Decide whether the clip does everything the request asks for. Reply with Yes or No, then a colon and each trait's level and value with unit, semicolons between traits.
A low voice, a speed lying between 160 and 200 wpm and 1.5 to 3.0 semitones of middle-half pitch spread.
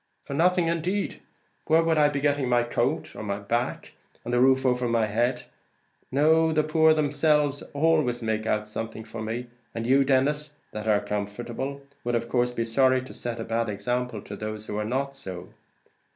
No: low, 125 Hz; average, 190 wpm; average, 4.5 semitones